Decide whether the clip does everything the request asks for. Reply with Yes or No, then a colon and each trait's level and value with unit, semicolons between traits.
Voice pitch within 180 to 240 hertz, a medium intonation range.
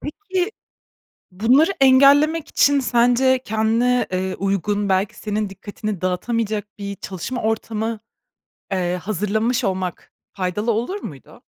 Yes: high, 220 Hz; average, 4.2 semitones